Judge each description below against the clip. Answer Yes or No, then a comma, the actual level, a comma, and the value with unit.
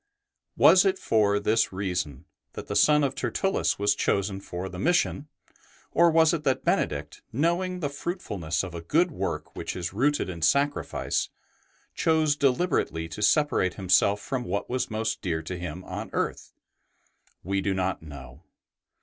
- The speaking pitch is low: Yes, low, 105 Hz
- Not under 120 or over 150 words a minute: No, average, 160 wpm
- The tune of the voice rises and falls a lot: Yes, wide, 8.5 semitones